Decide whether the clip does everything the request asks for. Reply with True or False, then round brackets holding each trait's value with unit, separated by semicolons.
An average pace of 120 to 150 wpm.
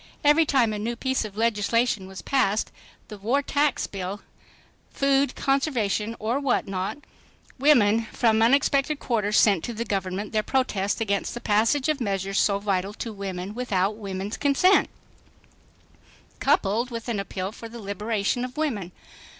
True (145 wpm)